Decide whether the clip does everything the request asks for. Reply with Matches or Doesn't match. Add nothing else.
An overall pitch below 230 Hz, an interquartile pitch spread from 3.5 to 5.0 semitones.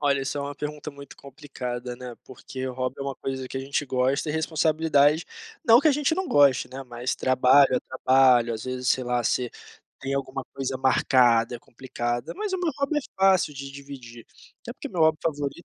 Doesn't match